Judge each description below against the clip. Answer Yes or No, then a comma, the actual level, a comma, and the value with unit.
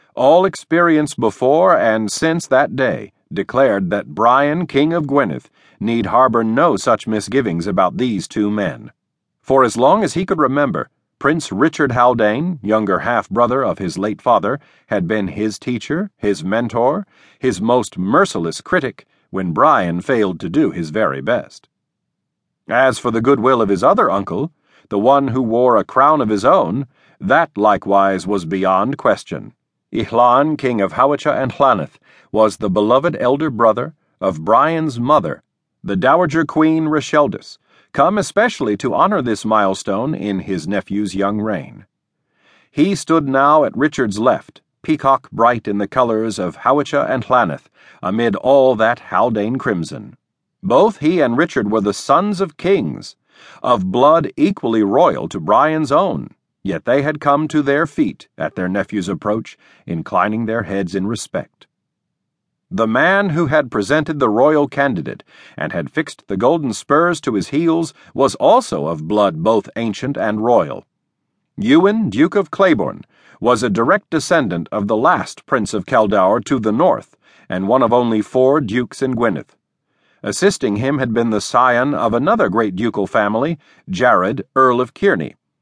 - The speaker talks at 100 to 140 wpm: No, average, 160 wpm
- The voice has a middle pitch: No, low, 130 Hz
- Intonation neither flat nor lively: No, wide, 6.4 semitones